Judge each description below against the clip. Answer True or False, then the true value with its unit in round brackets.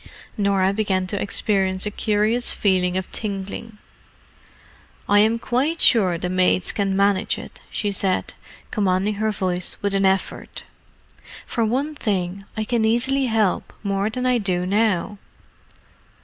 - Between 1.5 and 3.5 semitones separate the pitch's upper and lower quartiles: True (2.7 semitones)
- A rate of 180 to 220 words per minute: False (140 wpm)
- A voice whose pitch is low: False (200 Hz)